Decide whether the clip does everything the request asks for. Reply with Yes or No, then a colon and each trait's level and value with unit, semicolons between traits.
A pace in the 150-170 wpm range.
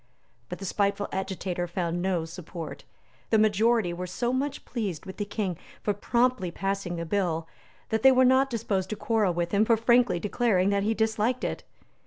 No: average, 185 wpm